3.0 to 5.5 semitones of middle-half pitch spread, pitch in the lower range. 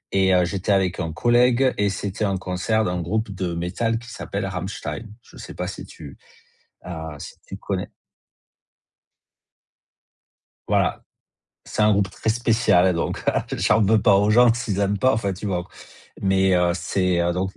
Yes: average, 3.3 semitones; low, 100 Hz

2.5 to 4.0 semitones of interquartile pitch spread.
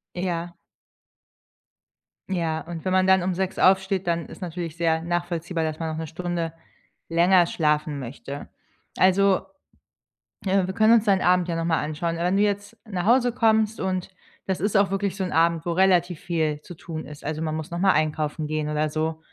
Yes: average, 2.9 semitones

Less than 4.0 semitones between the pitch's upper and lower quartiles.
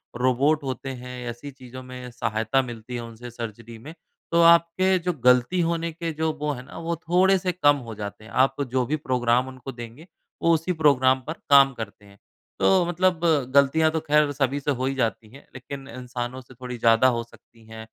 No: average, 4.6 semitones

